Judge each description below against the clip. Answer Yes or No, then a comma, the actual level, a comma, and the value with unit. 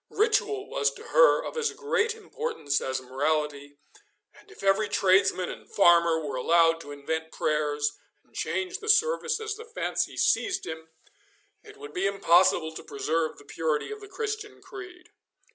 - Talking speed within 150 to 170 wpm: Yes, average, 160 wpm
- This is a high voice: Yes, high, 195 Hz